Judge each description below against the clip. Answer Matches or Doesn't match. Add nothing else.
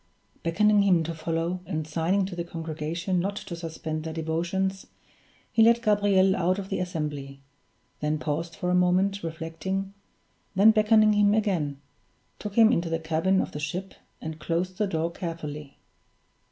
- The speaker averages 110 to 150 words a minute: Doesn't match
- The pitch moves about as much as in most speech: Matches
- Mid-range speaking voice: Matches